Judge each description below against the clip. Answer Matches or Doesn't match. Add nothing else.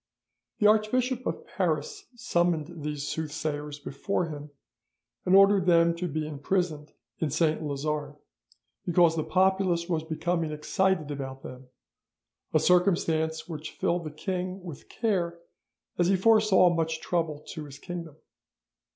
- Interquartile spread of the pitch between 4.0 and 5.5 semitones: Doesn't match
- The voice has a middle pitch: Matches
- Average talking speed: Doesn't match